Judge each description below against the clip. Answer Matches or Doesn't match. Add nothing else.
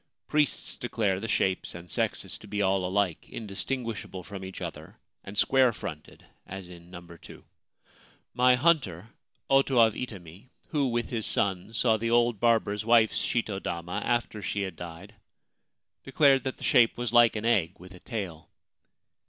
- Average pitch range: Matches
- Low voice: Matches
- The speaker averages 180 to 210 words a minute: Doesn't match